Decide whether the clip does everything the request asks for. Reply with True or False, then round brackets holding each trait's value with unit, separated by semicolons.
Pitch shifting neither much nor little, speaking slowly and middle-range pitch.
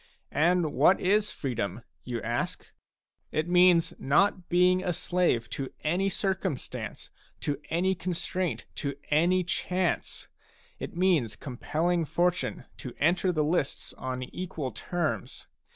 True (4.6 semitones; 125 wpm; 170 Hz)